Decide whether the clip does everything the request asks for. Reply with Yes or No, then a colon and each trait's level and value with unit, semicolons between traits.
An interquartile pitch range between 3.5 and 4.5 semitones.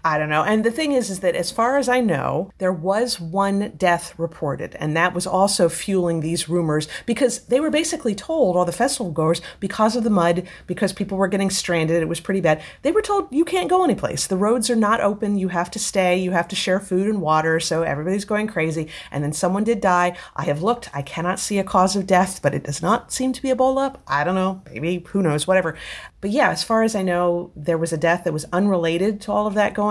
Yes: average, 4.2 semitones